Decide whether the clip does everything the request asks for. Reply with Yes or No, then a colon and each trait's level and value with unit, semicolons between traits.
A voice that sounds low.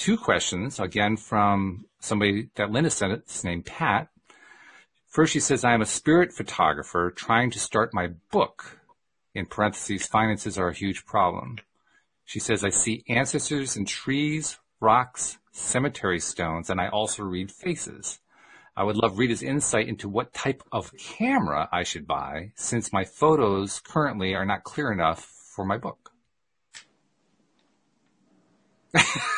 Yes: low, 105 Hz